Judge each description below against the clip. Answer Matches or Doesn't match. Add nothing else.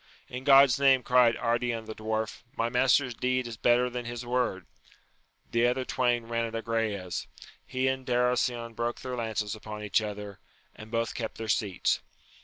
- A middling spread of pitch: Doesn't match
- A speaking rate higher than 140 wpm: Matches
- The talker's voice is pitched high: Doesn't match